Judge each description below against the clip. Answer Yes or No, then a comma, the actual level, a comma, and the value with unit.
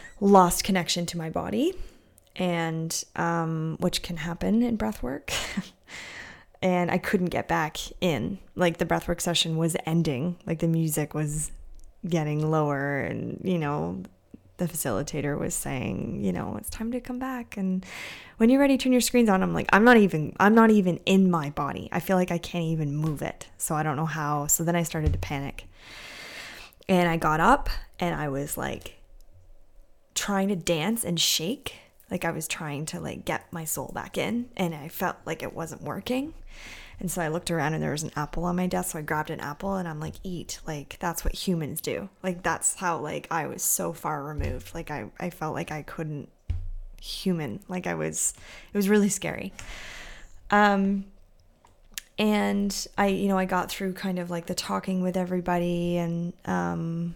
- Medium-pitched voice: Yes, medium, 175 Hz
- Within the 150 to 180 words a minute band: No, average, 190 wpm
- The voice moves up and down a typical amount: Yes, average, 3.4 semitones